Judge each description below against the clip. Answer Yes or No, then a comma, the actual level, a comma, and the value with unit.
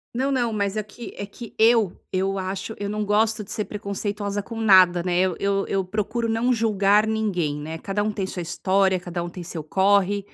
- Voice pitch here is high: Yes, high, 200 Hz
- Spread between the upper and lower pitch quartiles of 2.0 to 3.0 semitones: Yes, narrow, 2.4 semitones